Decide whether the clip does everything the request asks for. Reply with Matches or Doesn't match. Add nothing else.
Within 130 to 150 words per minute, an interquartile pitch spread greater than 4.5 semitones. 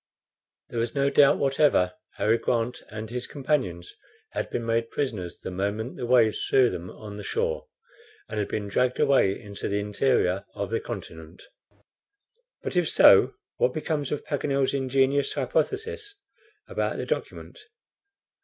Matches